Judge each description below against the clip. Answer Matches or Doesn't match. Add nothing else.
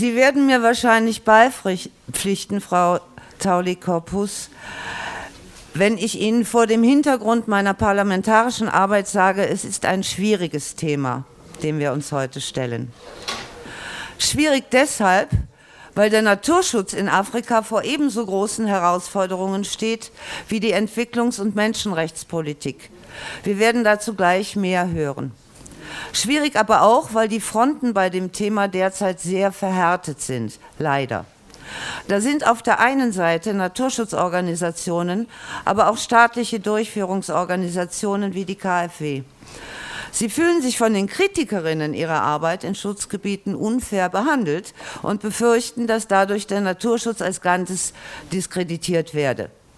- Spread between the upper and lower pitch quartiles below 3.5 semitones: Doesn't match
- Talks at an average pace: Doesn't match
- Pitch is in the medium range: Doesn't match